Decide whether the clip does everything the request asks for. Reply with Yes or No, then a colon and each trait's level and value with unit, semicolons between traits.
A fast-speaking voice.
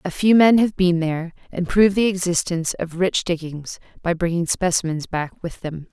No: average, 195 wpm